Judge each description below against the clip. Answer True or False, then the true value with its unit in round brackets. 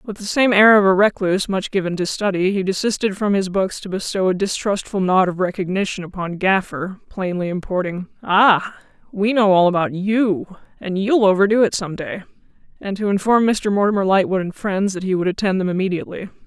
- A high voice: True (195 Hz)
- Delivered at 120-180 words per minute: False (195 wpm)